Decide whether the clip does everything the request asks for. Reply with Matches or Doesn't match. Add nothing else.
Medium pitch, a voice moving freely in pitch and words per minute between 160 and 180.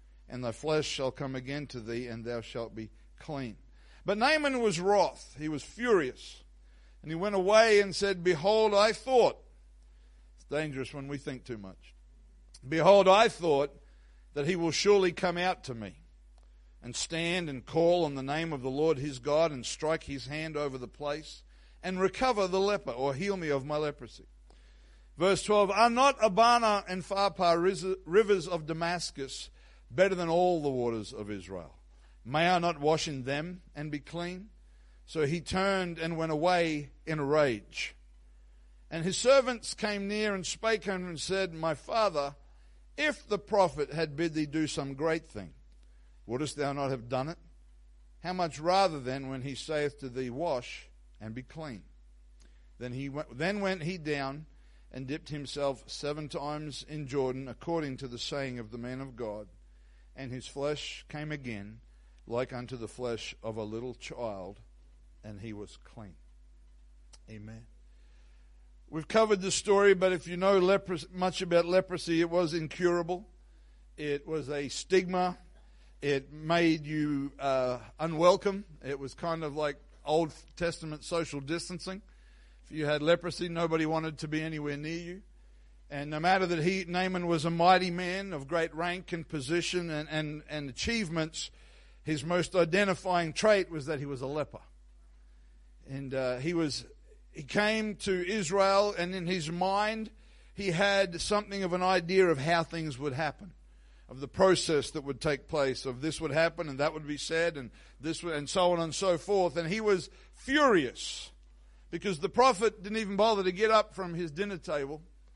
Matches